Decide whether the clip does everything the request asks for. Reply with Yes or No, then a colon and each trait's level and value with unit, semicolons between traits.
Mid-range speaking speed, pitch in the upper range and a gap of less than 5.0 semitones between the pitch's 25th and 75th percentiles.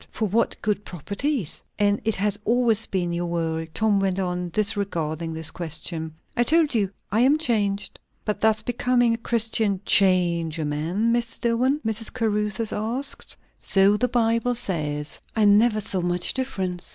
Yes: average, 160 wpm; high, 205 Hz; average, 4.6 semitones